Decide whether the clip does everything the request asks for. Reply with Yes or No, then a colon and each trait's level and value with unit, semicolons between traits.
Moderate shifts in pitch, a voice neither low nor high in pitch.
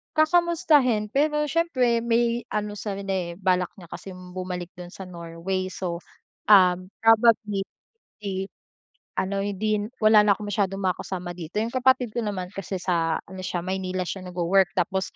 No: average, 3.4 semitones; high, 195 Hz